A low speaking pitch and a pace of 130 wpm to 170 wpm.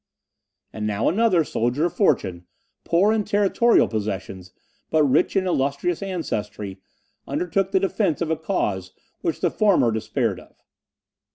No: medium, 160 Hz; average, 140 wpm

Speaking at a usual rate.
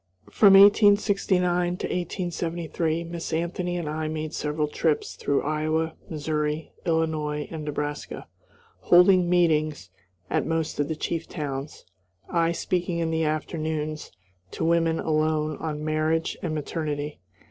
No: slow, 125 wpm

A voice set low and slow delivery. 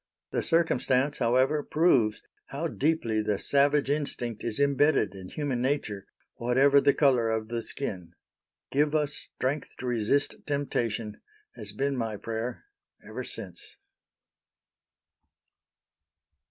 Yes: low, 130 Hz; slow, 115 wpm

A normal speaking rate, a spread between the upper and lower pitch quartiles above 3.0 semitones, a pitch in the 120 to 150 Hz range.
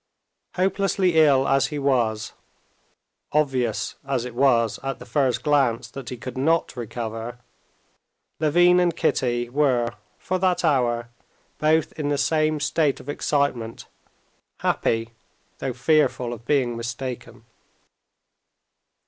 No: slow, 120 wpm; average, 4.1 semitones; low, 135 Hz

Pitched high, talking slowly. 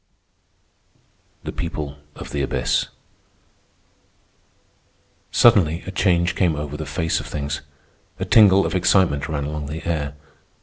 No: very low, 80 Hz; slow, 125 wpm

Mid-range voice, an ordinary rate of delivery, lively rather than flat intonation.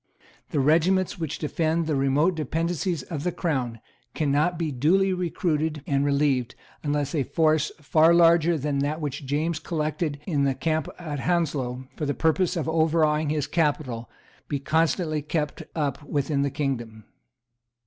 No: medium, 150 Hz; average, 150 wpm; average, 2.7 semitones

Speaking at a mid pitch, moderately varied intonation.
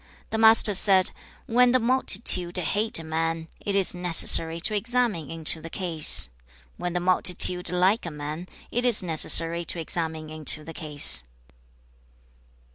Yes: medium, 175 Hz; average, 4.0 semitones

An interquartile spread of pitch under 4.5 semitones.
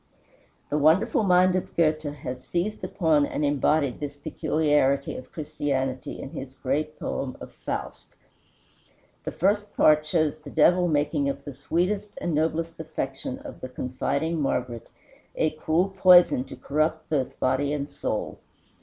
Yes: average, 3.3 semitones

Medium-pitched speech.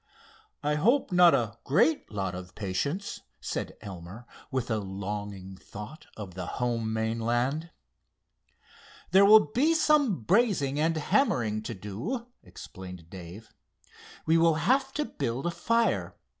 No: low, 120 Hz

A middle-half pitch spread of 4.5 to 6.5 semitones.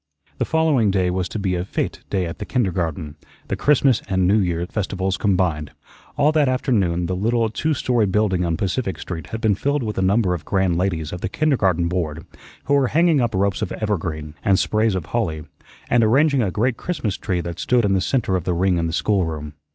Yes: average, 5.0 semitones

